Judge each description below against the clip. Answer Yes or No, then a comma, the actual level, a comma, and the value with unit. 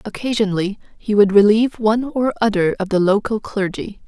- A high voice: Yes, high, 210 Hz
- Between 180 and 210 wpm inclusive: No, average, 160 wpm